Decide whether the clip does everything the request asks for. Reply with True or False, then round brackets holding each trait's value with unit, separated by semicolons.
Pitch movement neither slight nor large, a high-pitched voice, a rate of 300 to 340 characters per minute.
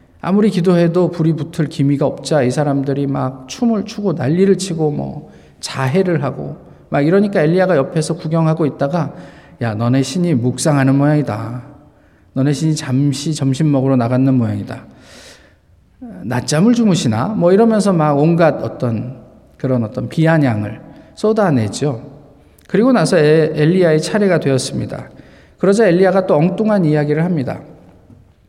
False (4.9 semitones; 150 Hz; 320 characters per minute)